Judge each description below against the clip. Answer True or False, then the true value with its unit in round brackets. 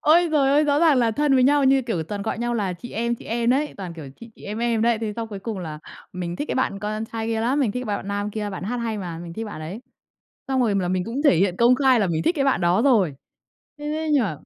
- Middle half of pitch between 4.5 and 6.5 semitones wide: True (5.0 semitones)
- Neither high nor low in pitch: False (225 Hz)